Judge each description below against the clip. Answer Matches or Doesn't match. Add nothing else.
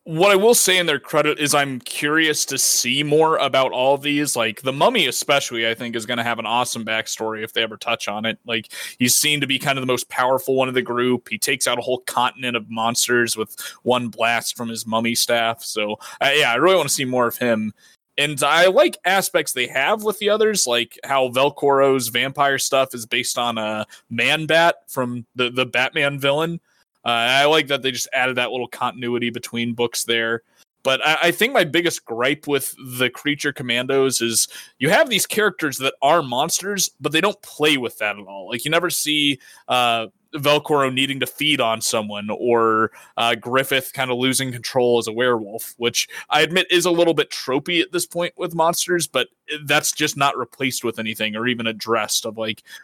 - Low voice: Matches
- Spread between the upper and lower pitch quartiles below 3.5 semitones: Doesn't match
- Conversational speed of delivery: Doesn't match